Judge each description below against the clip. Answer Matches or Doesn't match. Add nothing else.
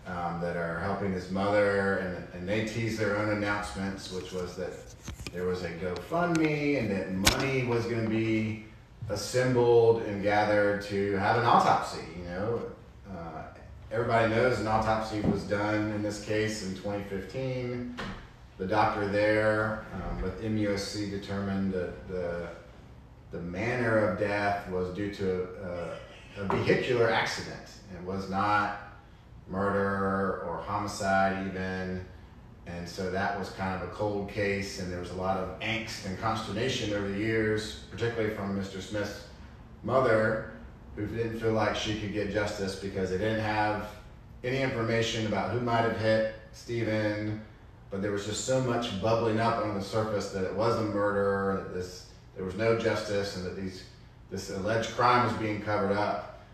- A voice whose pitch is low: Matches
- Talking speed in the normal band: Matches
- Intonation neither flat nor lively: Doesn't match